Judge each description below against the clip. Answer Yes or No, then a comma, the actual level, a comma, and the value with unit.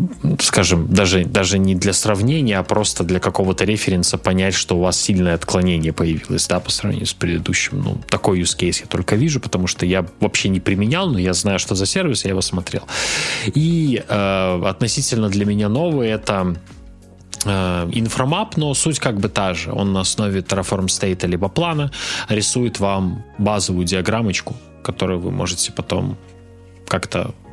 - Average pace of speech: No, fast, 165 wpm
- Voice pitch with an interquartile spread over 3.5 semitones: No, average, 3.0 semitones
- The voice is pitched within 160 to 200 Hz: No, very low, 95 Hz